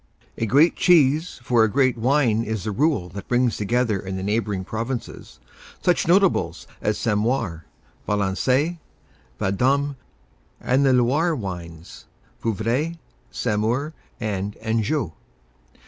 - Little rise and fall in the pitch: No, average, 5.0 semitones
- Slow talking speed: Yes, slow, 120 wpm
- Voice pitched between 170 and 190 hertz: No, low, 115 Hz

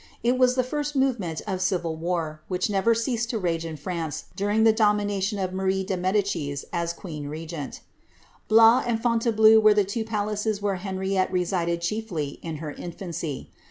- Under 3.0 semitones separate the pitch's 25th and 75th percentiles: No, average, 4.5 semitones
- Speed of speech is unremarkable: Yes, average, 170 wpm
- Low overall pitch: No, high, 195 Hz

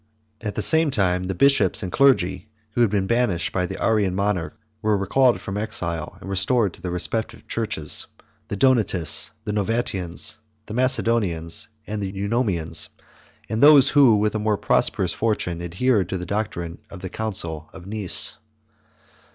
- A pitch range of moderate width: Yes, average, 3.9 semitones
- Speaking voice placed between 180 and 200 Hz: No, low, 100 Hz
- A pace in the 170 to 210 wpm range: No, average, 160 wpm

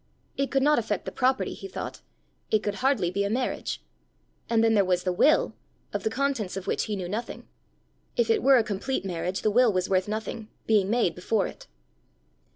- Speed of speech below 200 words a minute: No, fast, 205 wpm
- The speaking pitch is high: Yes, high, 215 Hz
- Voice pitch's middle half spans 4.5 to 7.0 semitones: Yes, average, 4.8 semitones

